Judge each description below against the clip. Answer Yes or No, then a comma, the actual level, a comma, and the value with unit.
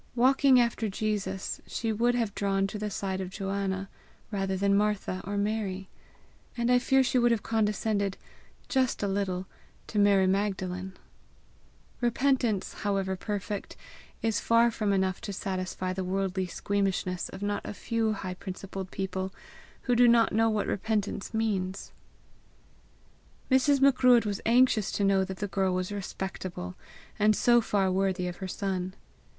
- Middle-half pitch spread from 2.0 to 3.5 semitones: Yes, average, 2.8 semitones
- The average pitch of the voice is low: No, high, 200 Hz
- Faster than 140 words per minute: Yes, average, 150 wpm